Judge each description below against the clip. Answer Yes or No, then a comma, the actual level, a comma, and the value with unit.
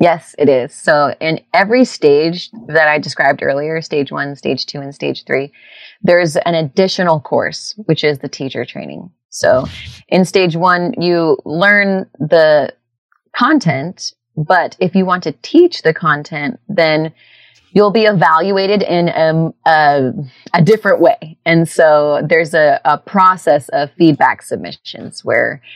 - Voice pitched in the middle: Yes, medium, 165 Hz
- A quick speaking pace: No, average, 145 wpm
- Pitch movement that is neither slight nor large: Yes, average, 3.9 semitones